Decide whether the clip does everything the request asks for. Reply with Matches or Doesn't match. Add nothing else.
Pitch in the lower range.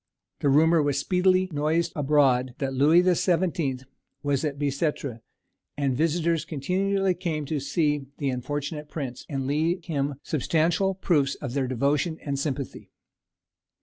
Doesn't match